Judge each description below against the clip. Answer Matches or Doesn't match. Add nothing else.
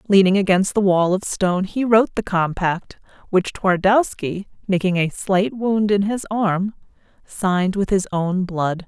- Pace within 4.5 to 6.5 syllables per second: Doesn't match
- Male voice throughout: Doesn't match